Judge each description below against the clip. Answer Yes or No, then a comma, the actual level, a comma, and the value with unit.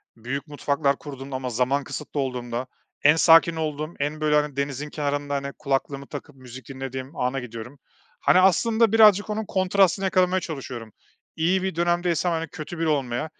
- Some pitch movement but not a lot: Yes, average, 4.3 semitones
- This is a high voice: No, medium, 145 Hz